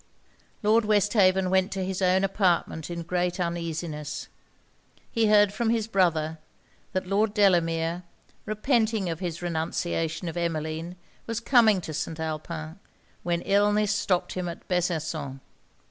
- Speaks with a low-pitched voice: No, medium, 180 Hz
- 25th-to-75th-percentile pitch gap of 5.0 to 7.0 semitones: No, average, 3.8 semitones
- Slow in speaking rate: Yes, slow, 130 wpm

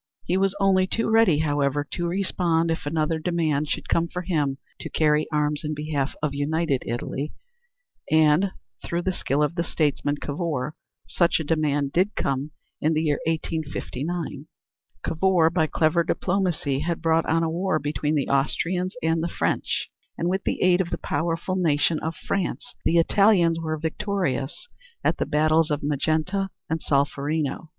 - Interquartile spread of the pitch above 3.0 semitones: No, average, 2.7 semitones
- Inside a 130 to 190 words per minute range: Yes, average, 165 wpm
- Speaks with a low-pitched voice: No, medium, 160 Hz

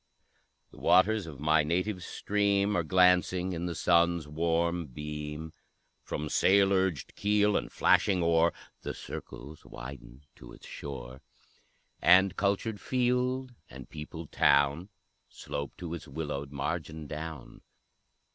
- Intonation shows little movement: No, average, 4.1 semitones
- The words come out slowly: Yes, slow, 125 wpm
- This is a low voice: Yes, very low, 85 Hz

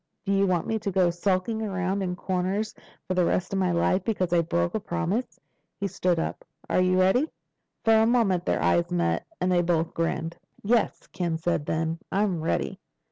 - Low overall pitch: No, medium, 185 Hz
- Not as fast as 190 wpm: No, average, 195 wpm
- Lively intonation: No, average, 2.9 semitones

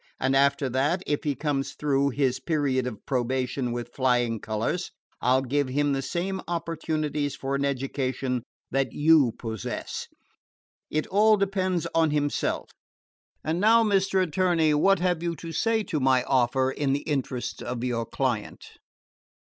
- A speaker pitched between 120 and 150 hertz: Yes, medium, 140 Hz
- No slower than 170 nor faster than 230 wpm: No, average, 155 wpm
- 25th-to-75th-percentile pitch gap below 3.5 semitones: No, average, 4.3 semitones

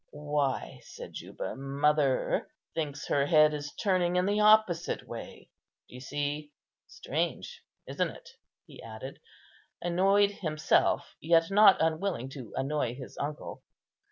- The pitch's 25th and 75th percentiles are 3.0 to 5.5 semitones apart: Yes, average, 4.1 semitones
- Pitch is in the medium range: Yes, medium, 150 Hz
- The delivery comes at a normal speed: No, slow, 125 wpm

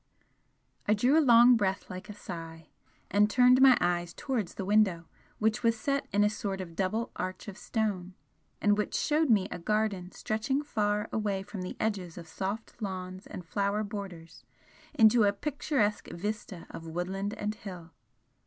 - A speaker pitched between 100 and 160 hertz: No, high, 205 Hz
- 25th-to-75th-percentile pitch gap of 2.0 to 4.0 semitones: Yes, average, 3.0 semitones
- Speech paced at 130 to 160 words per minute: No, average, 170 wpm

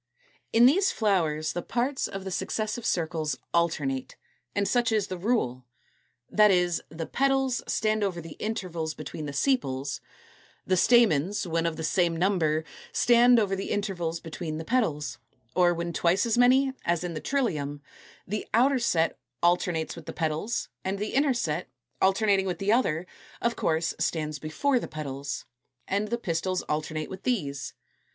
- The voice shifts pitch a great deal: Yes, wide, 5.7 semitones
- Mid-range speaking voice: Yes, medium, 180 Hz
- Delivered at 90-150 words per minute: No, average, 165 wpm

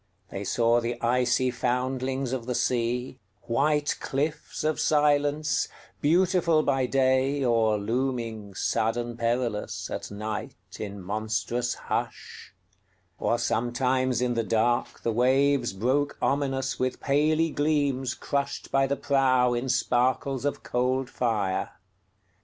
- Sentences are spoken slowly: Yes, slow, 105 wpm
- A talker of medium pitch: No, low, 125 Hz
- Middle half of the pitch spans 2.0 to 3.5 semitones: Yes, average, 2.8 semitones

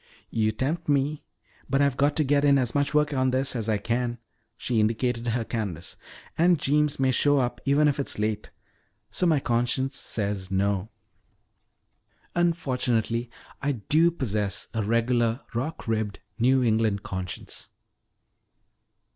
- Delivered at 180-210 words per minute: No, average, 145 wpm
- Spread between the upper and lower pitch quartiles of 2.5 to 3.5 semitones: No, average, 4.3 semitones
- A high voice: No, low, 125 Hz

